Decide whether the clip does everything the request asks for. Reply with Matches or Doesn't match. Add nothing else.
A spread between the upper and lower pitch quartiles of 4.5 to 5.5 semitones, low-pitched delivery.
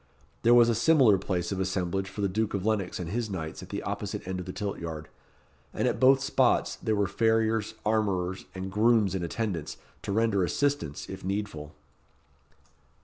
Doesn't match